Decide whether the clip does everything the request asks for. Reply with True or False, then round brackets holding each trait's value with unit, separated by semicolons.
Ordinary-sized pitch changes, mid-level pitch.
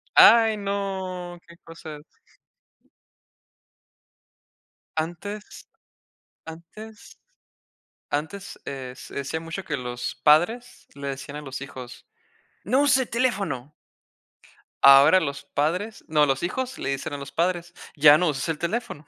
False (5.9 semitones; 165 Hz)